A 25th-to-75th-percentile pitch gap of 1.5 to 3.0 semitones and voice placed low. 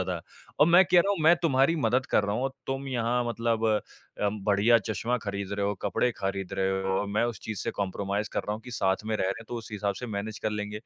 No: average, 3.4 semitones; low, 110 Hz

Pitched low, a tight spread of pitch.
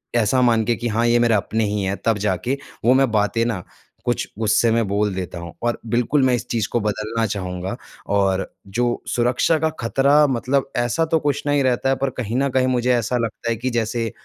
No: low, 115 Hz; average, 3.1 semitones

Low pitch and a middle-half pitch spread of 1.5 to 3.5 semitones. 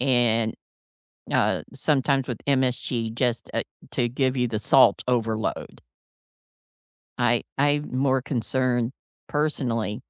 Yes: low, 125 Hz; narrow, 2.5 semitones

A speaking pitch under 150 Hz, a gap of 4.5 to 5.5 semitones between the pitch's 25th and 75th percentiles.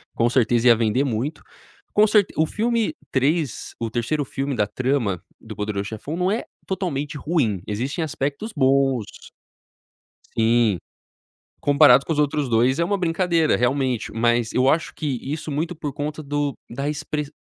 Yes: medium, 140 Hz; average, 4.8 semitones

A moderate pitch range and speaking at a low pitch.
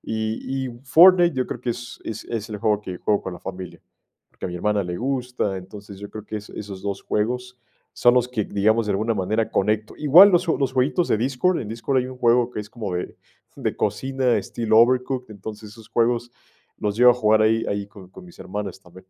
Yes: average, 3.5 semitones; low, 110 Hz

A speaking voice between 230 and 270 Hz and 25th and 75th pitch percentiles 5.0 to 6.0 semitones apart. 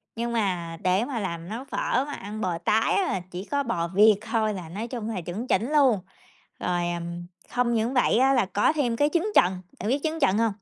No: high, 220 Hz; wide, 5.4 semitones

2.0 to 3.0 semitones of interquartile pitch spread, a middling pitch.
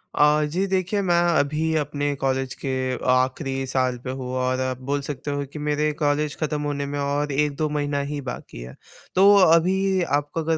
Yes: narrow, 2.5 semitones; medium, 145 Hz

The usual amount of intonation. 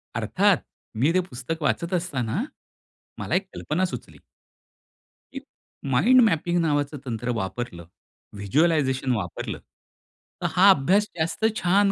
No: wide, 6.8 semitones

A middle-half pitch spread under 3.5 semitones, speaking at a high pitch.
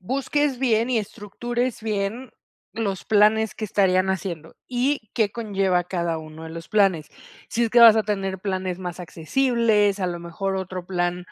No: average, 3.8 semitones; high, 200 Hz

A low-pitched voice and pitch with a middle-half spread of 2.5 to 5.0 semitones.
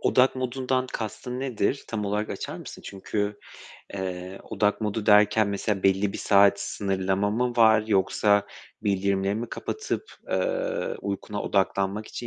Yes: low, 105 Hz; average, 2.9 semitones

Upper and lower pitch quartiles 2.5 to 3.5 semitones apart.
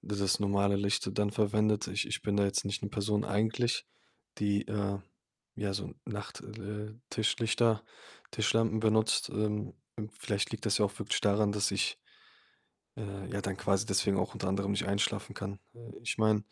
No: narrow, 1.3 semitones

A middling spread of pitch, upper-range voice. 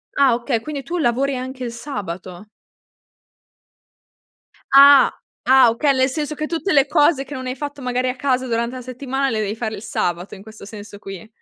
Yes: average, 3.8 semitones; very high, 255 Hz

